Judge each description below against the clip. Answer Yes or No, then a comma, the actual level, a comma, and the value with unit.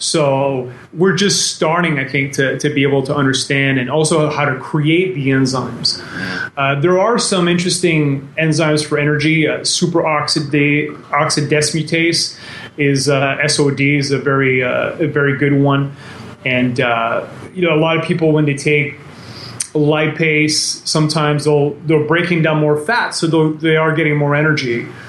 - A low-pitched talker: No, medium, 150 Hz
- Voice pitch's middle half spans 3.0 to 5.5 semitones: No, narrow, 2.4 semitones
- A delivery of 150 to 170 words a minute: Yes, average, 155 wpm